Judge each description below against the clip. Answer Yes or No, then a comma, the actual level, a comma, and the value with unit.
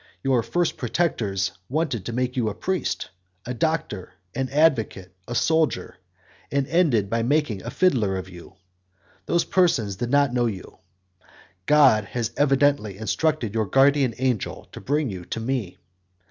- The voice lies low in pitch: Yes, low, 125 Hz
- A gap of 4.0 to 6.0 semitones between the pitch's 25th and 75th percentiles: Yes, average, 5.2 semitones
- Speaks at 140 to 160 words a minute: Yes, average, 150 wpm